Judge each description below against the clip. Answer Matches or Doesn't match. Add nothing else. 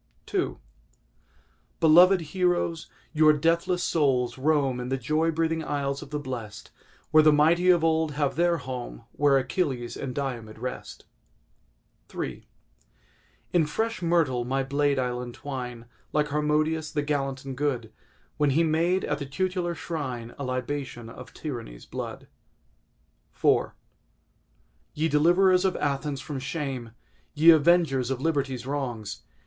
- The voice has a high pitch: Doesn't match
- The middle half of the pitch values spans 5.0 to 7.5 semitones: Doesn't match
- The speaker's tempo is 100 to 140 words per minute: Matches